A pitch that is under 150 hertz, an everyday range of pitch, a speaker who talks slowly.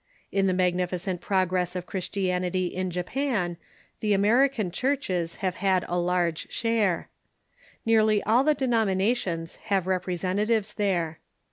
No: high, 190 Hz; average, 3.3 semitones; slow, 125 wpm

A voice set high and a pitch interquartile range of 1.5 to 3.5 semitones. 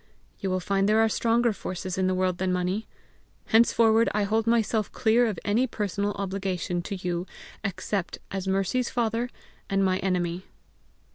Yes: high, 200 Hz; average, 3.2 semitones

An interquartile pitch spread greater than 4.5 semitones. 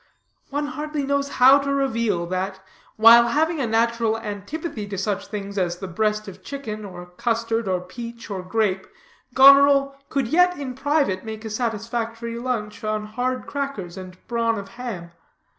Yes: average, 5.0 semitones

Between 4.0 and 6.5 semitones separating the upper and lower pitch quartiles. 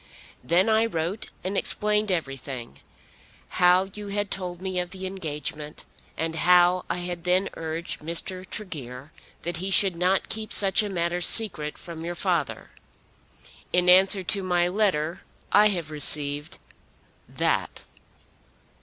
No: average, 3.0 semitones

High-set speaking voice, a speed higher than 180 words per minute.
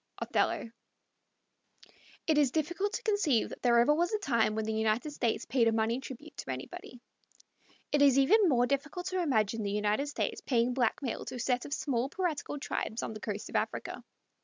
Yes: very high, 255 Hz; average, 190 wpm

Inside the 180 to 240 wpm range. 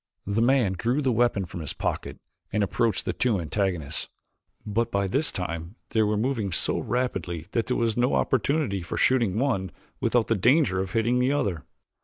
Yes: average, 185 wpm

